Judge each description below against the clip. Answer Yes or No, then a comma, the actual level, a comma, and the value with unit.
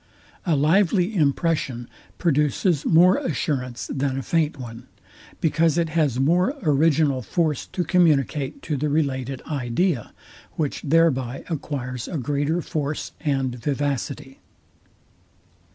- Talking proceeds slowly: Yes, slow, 115 wpm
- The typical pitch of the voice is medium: Yes, medium, 145 Hz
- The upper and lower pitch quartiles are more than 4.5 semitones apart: No, average, 3.6 semitones